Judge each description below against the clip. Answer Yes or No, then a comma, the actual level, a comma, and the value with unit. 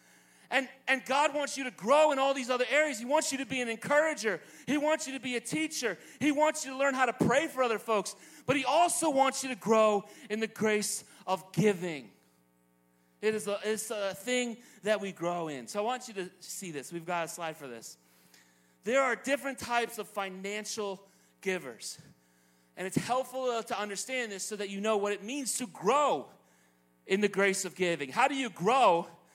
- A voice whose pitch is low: No, high, 215 Hz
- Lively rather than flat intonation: Yes, wide, 6.5 semitones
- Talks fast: Yes, fast, 210 wpm